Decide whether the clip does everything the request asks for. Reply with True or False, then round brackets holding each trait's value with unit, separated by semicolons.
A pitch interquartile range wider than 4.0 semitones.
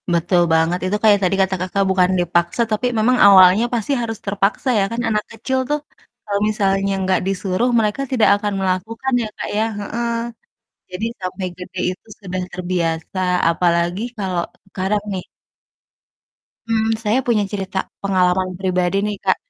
False (2.7 semitones)